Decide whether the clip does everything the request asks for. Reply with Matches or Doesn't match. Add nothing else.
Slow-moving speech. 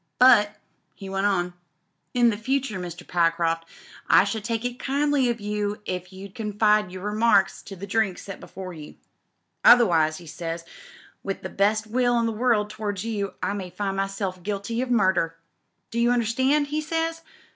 Doesn't match